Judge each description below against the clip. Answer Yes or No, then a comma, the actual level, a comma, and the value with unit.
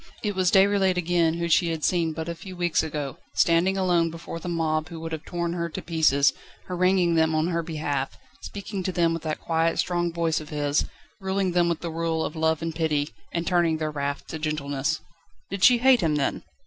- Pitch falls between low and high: Yes, medium, 165 Hz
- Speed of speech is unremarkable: No, fast, 215 wpm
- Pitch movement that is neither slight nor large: No, narrow, 2.0 semitones